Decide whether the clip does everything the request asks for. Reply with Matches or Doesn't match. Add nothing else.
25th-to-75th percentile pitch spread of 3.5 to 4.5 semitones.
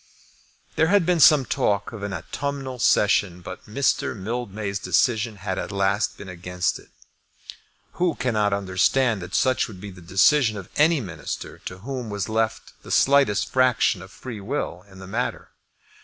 Doesn't match